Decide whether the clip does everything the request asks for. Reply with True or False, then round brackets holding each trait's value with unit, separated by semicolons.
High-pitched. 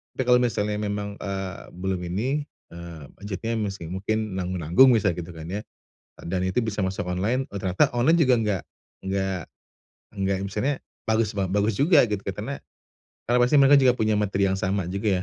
False (100 Hz)